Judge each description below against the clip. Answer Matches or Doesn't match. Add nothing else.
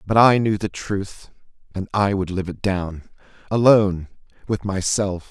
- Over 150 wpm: Doesn't match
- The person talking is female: Doesn't match